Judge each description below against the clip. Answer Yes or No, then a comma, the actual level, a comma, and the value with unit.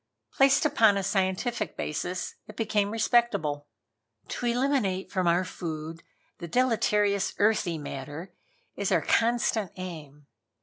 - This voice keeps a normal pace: No, slow, 120 wpm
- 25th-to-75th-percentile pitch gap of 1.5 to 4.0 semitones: No, average, 5.0 semitones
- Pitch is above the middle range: Yes, high, 195 Hz